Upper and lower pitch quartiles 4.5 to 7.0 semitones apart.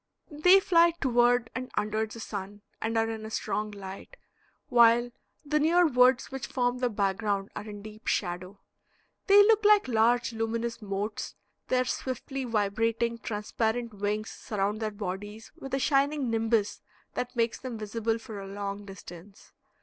No: average, 3.4 semitones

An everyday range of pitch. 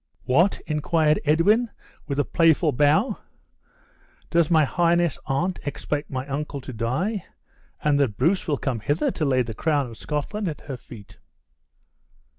Yes: average, 3.8 semitones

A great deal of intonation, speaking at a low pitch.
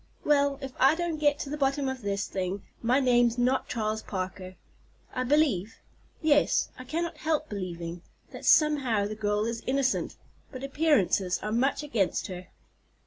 No: wide, 5.9 semitones; very high, 250 Hz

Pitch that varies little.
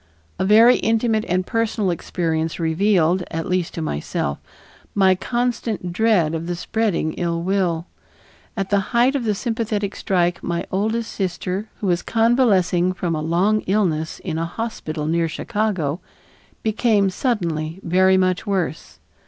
No: average, 4.3 semitones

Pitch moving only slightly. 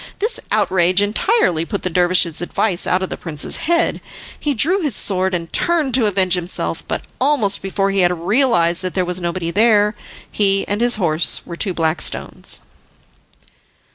No: average, 4.2 semitones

